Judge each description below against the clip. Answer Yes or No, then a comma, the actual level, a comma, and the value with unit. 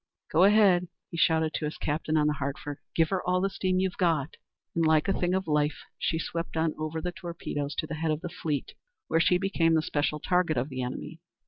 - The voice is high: No, medium, 160 Hz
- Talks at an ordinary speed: No, fast, 230 wpm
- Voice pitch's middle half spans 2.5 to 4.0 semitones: Yes, average, 2.9 semitones